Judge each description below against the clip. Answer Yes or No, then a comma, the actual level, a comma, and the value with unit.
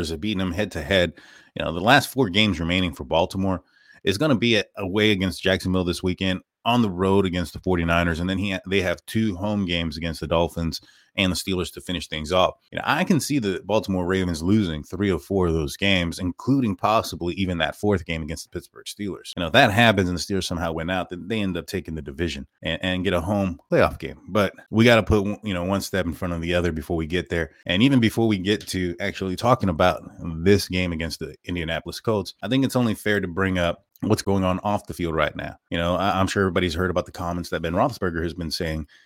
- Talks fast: Yes, fast, 250 wpm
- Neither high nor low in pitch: No, very low, 95 Hz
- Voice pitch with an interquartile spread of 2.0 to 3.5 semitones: Yes, average, 2.9 semitones